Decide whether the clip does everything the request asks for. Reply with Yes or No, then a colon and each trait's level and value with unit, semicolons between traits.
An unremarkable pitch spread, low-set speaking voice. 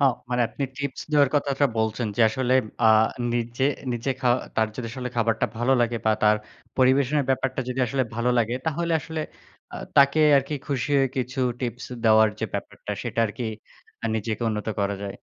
Yes: average, 3.1 semitones; low, 125 Hz